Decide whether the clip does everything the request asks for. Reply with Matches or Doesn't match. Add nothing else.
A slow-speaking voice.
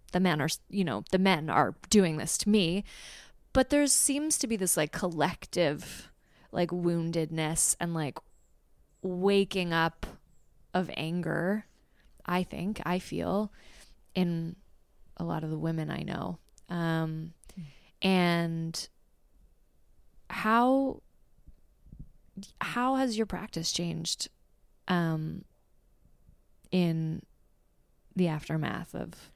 Matches